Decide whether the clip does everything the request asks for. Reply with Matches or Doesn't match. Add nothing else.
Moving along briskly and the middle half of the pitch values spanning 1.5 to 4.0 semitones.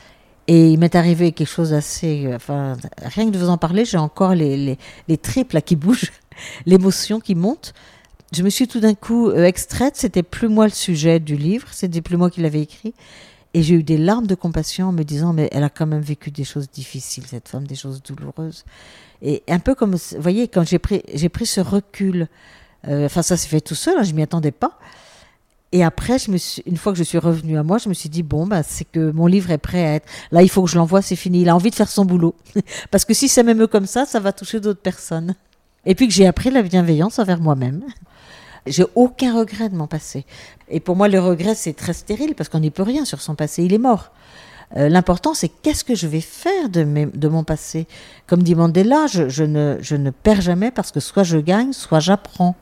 Doesn't match